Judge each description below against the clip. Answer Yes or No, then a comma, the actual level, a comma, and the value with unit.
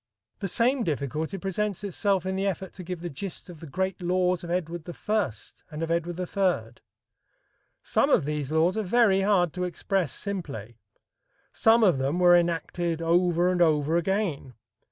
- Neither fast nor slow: Yes, average, 170 wpm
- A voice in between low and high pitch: Yes, medium, 175 Hz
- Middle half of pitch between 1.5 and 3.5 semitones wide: Yes, average, 2.9 semitones